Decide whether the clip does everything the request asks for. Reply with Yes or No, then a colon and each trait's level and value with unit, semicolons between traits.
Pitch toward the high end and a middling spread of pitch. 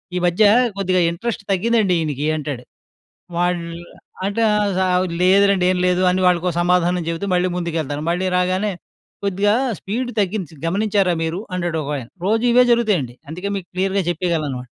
No: medium, 180 Hz; average, 3.0 semitones